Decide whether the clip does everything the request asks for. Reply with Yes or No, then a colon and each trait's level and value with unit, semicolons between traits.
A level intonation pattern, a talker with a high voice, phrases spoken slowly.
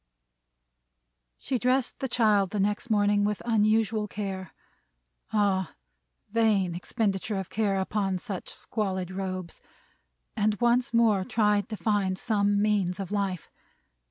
Yes: narrow, 2.3 semitones; high, 205 Hz; slow, 120 wpm